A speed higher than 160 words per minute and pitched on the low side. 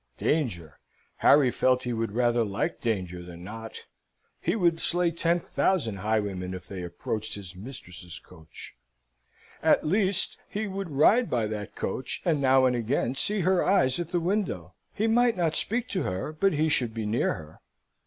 Yes: average, 175 wpm; low, 125 Hz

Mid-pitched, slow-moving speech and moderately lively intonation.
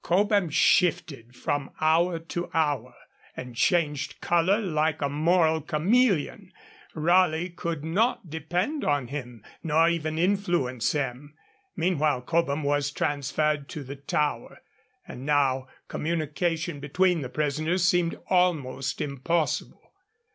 Yes: medium, 155 Hz; slow, 115 wpm; average, 3.4 semitones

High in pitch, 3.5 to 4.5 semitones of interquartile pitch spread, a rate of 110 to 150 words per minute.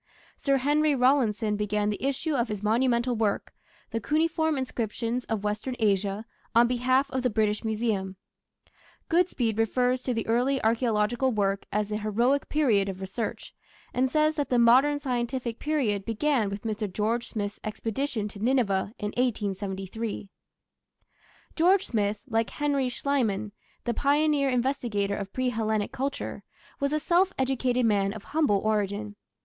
Yes: high, 235 Hz; average, 4.2 semitones; average, 145 wpm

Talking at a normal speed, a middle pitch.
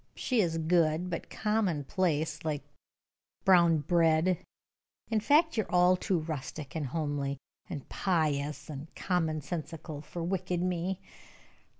No: slow, 125 wpm; medium, 165 Hz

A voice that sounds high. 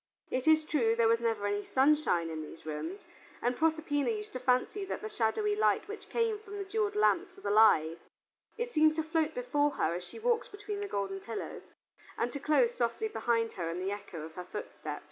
Yes: very high, 285 Hz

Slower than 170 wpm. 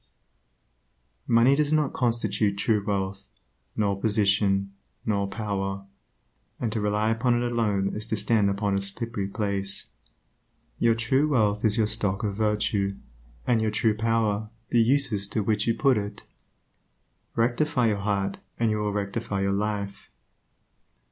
Yes: average, 145 wpm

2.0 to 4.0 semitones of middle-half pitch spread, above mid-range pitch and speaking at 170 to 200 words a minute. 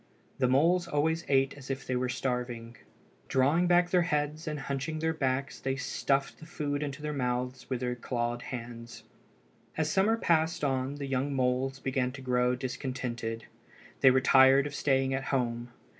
No: average, 2.8 semitones; low, 135 Hz; average, 175 wpm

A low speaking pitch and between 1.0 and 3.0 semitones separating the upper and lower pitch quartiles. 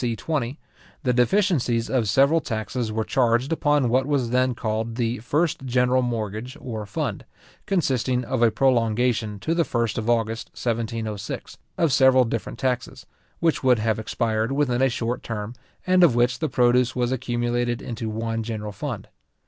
Yes: low, 120 Hz; narrow, 2.5 semitones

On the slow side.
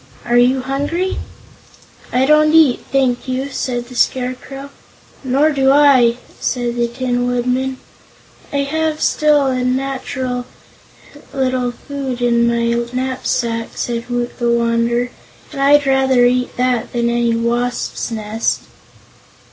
Yes: slow, 125 wpm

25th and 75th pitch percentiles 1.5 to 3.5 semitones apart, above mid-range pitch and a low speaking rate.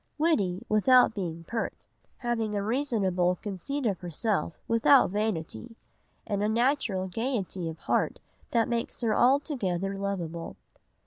No: average, 4.7 semitones; high, 210 Hz; slow, 125 wpm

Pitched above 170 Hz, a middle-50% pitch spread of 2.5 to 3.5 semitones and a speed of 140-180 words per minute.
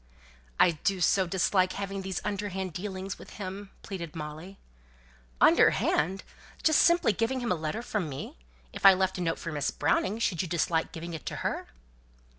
Yes: high, 190 Hz; average, 3.0 semitones; average, 175 wpm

